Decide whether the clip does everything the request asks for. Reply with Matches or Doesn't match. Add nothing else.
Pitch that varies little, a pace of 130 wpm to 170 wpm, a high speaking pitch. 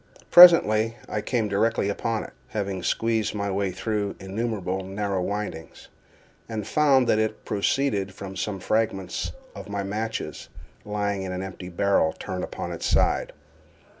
Doesn't match